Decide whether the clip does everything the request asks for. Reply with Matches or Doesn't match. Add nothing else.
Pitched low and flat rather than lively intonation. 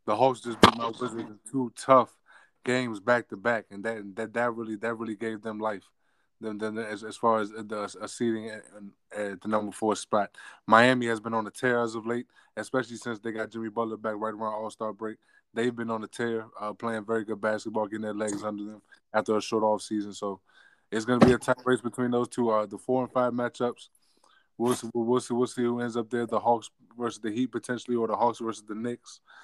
Matches